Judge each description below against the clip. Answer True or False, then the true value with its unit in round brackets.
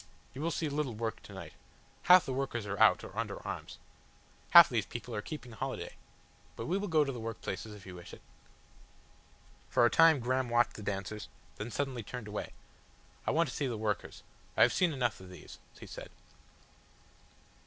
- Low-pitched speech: True (120 Hz)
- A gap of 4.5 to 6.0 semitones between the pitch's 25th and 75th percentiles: True (5.3 semitones)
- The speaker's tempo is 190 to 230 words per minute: True (195 wpm)